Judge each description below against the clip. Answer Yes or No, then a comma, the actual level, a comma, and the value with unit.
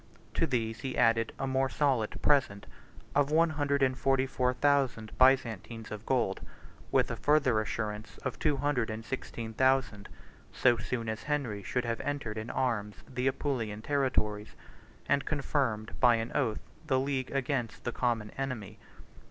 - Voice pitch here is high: No, low, 125 Hz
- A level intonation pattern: No, average, 3.5 semitones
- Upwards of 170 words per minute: No, average, 160 wpm